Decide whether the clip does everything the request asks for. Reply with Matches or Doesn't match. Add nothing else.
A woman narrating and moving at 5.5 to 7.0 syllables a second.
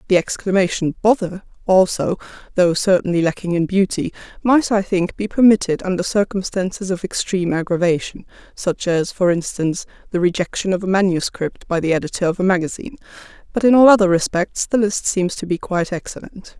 Matches